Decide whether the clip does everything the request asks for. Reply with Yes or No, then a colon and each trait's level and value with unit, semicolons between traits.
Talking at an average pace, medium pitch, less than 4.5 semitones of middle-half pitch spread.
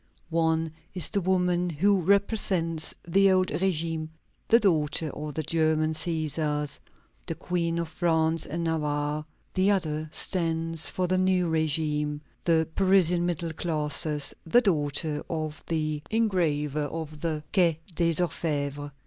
No: slow, 130 wpm; medium, 160 Hz; narrow, 2.6 semitones